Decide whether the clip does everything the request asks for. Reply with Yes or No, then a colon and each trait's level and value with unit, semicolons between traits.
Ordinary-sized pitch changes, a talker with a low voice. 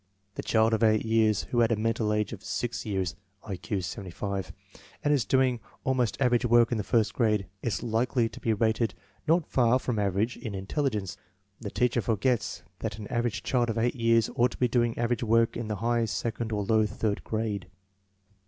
No: narrow, 2.2 semitones; low, 115 Hz